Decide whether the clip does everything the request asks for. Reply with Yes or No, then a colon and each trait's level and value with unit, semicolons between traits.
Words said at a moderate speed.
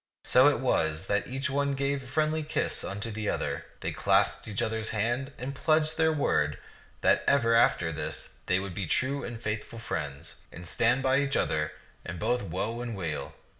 Yes: average, 190 wpm